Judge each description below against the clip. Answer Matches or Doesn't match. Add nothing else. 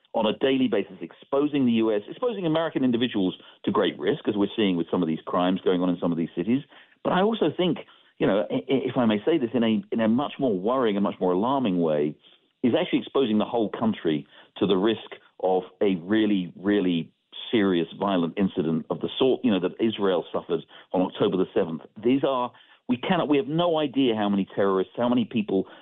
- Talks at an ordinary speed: Doesn't match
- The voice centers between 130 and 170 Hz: Doesn't match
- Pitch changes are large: Matches